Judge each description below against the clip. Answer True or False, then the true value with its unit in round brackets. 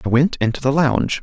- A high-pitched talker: False (135 Hz)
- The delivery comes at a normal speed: False (245 wpm)